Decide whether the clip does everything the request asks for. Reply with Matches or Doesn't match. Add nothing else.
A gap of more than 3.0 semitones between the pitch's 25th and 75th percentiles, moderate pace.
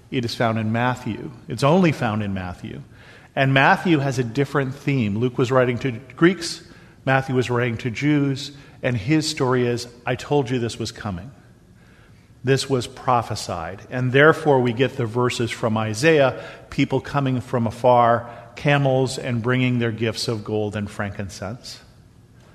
Doesn't match